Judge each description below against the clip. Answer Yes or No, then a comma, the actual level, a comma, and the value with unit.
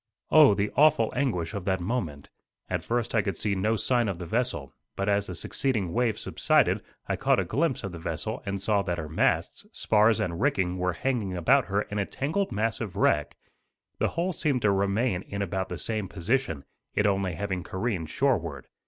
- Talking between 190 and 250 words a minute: Yes, average, 200 wpm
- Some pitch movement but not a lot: Yes, average, 4.8 semitones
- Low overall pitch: Yes, low, 100 Hz